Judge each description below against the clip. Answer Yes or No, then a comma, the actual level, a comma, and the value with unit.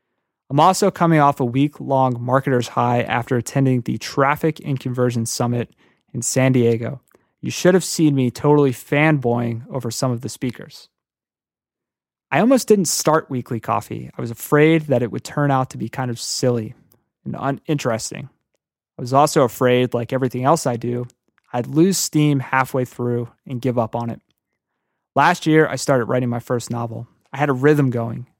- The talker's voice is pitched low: Yes, low, 130 Hz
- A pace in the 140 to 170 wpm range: No, average, 180 wpm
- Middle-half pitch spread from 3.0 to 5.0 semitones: Yes, average, 3.3 semitones